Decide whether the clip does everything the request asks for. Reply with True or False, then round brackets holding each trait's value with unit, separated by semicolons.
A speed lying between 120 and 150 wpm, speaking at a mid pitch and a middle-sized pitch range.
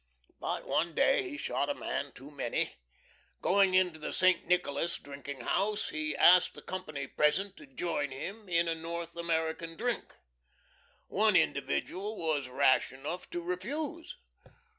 True (145 wpm; 170 Hz; 4.4 semitones)